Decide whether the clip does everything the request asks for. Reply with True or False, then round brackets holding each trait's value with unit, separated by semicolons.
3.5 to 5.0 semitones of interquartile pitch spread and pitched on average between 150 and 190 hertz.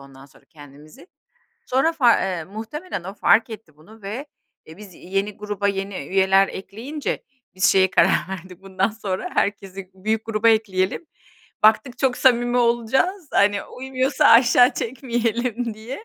False (4.1 semitones; 215 Hz)